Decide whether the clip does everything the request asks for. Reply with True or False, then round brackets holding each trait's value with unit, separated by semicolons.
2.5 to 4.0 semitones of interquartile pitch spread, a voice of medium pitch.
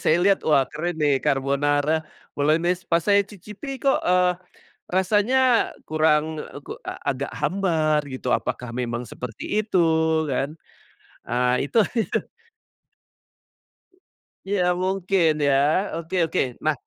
False (4.8 semitones; 160 Hz)